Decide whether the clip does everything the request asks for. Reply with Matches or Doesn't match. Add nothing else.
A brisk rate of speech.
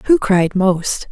Doesn't match